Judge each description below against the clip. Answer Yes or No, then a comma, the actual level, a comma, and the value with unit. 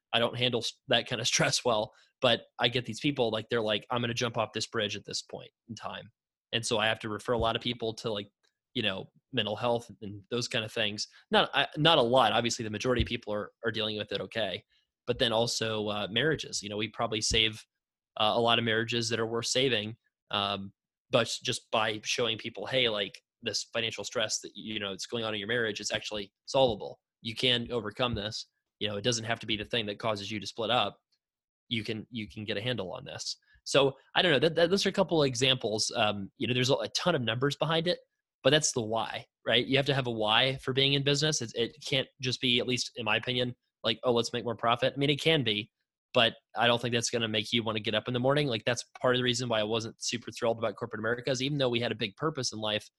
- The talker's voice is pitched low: Yes, low, 115 Hz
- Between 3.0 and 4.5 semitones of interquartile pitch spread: No, narrow, 2.5 semitones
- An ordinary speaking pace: No, fast, 265 wpm